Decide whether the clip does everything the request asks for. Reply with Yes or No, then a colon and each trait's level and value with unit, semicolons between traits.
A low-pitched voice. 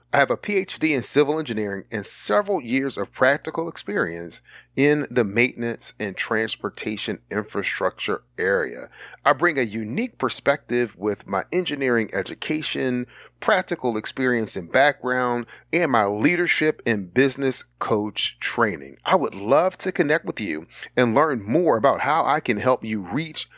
Yes: low, 125 Hz